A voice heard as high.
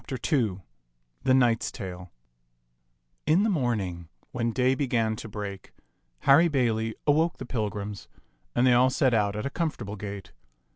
No: low, 115 Hz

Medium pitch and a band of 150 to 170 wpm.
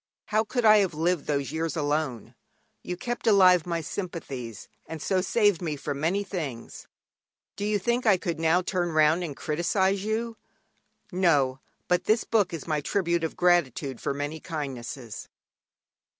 Yes: medium, 170 Hz; average, 160 wpm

